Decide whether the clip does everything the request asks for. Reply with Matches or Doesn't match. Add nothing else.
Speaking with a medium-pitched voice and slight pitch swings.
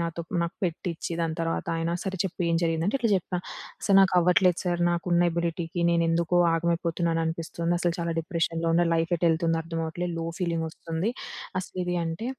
Matches